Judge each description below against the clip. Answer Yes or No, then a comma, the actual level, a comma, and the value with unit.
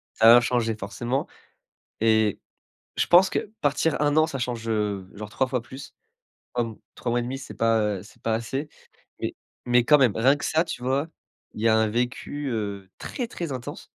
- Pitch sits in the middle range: No, low, 120 Hz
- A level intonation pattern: No, average, 3.8 semitones